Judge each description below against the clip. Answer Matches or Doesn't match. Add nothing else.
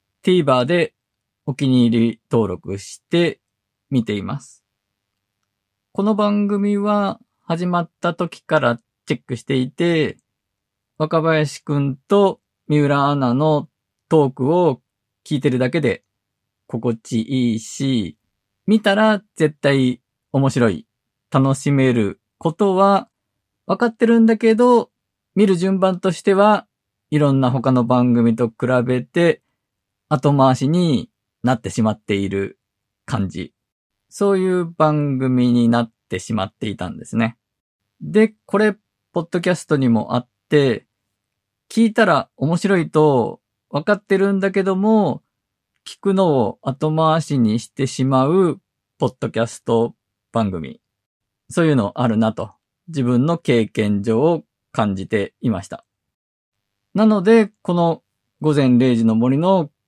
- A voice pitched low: Matches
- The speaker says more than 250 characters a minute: Doesn't match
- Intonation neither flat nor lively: Doesn't match